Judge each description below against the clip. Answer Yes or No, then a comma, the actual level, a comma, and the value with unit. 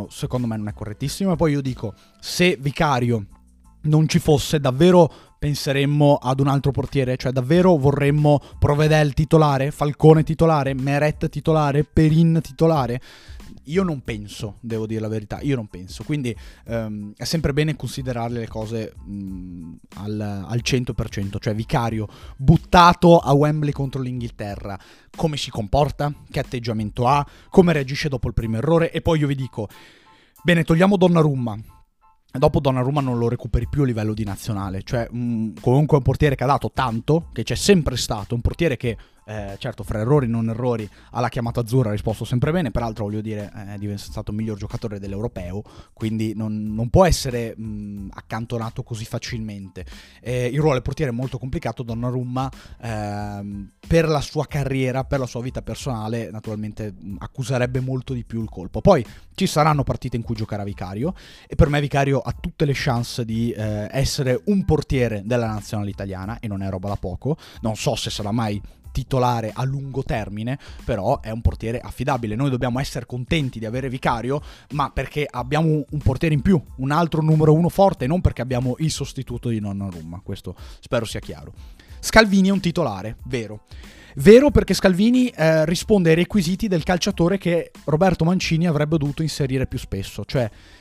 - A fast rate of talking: Yes, fast, 175 wpm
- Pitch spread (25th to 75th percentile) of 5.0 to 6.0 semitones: Yes, wide, 5.4 semitones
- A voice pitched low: Yes, low, 125 Hz